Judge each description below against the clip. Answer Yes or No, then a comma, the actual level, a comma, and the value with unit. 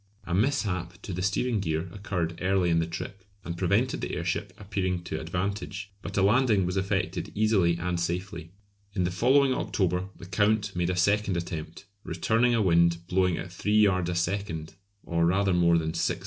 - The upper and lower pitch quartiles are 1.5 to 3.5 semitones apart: Yes, average, 3.0 semitones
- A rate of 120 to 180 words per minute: No, average, 200 wpm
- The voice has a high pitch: No, very low, 90 Hz